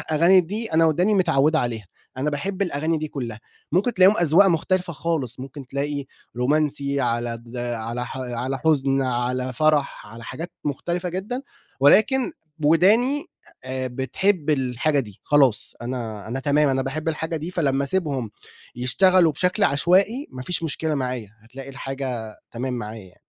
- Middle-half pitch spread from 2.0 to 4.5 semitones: No, average, 5.2 semitones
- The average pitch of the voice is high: No, medium, 140 Hz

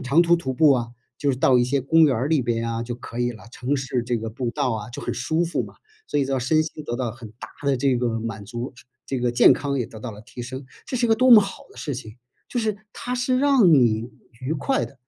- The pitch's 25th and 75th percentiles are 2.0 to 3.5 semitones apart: No, average, 4.7 semitones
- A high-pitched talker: No, low, 130 Hz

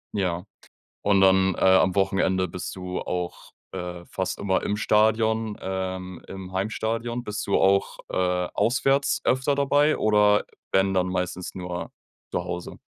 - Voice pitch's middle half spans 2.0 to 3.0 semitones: Yes, average, 2.7 semitones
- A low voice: Yes, very low, 95 Hz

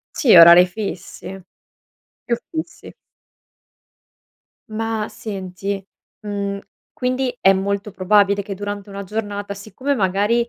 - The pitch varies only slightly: Yes, narrow, 2.1 semitones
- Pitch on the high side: Yes, high, 200 Hz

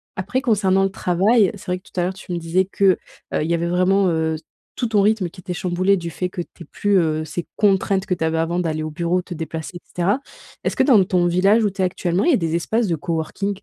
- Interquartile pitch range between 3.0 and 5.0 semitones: No, narrow, 2.6 semitones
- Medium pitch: Yes, medium, 180 Hz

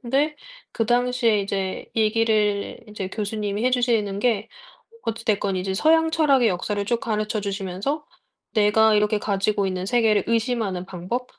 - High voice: Yes, high, 215 Hz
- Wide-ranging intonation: No, average, 3.1 semitones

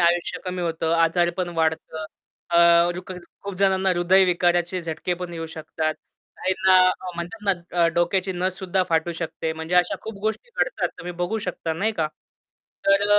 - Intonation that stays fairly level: Yes, narrow, 2.2 semitones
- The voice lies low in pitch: No, medium, 175 Hz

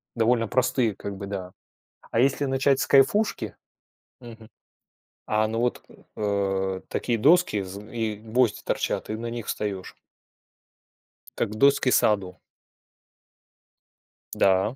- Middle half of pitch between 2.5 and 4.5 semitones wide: Yes, average, 3.7 semitones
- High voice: No, low, 110 Hz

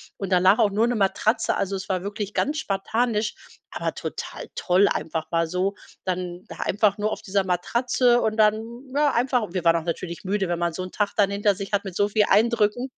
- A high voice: Yes, high, 200 Hz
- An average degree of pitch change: Yes, average, 3.1 semitones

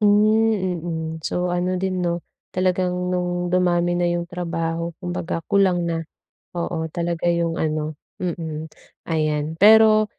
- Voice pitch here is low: No, medium, 175 Hz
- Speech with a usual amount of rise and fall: No, narrow, 1.8 semitones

